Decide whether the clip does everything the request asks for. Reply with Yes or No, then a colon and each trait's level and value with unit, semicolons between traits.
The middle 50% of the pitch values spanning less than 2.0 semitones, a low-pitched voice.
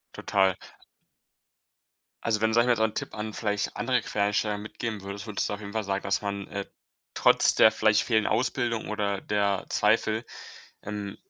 Yes: narrow, 1.6 semitones; low, 105 Hz